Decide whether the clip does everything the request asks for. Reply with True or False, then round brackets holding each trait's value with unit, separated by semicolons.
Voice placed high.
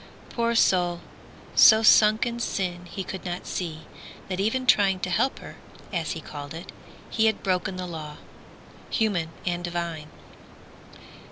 False (180 Hz)